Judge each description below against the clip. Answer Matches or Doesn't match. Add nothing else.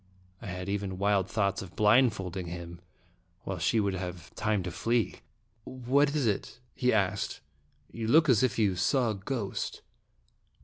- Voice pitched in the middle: Doesn't match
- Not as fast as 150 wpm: Doesn't match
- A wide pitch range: Doesn't match